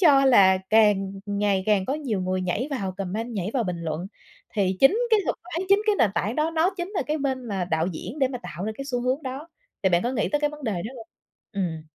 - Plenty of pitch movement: Yes, wide, 6.8 semitones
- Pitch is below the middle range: No, high, 225 Hz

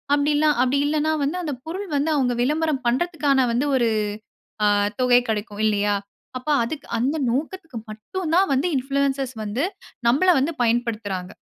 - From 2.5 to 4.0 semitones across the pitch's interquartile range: No, average, 4.4 semitones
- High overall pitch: Yes, very high, 270 Hz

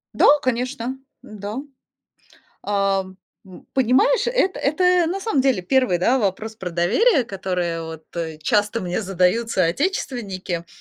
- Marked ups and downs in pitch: Yes, wide, 6.4 semitones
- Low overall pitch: No, high, 210 Hz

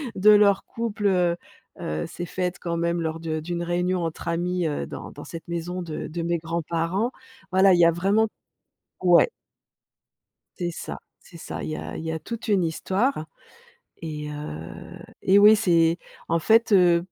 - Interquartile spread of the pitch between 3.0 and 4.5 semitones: No, narrow, 2.5 semitones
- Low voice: No, medium, 175 Hz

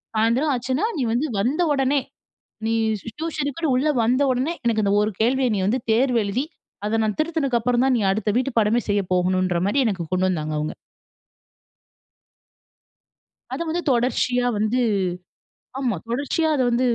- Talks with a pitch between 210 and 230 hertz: No, high, 245 Hz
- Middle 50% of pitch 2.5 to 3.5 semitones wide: No, average, 4.3 semitones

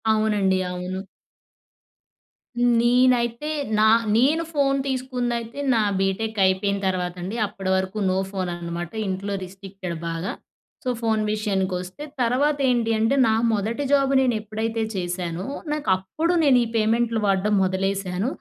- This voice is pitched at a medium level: No, high, 215 Hz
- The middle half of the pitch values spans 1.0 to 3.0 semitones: No, average, 4.2 semitones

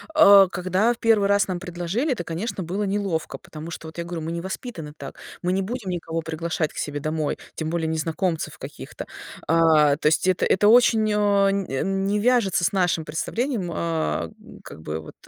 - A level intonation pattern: No, average, 3.9 semitones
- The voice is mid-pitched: Yes, medium, 175 Hz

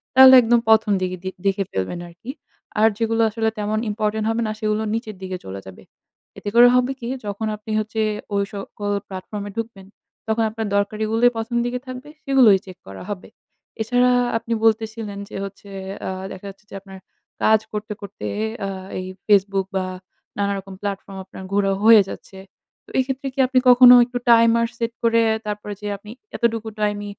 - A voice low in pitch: No, high, 215 Hz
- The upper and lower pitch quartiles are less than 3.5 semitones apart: Yes, narrow, 2.4 semitones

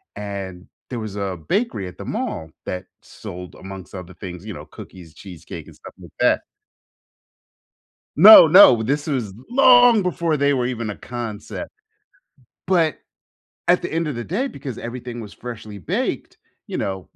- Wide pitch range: Yes, wide, 8.2 semitones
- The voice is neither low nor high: No, low, 115 Hz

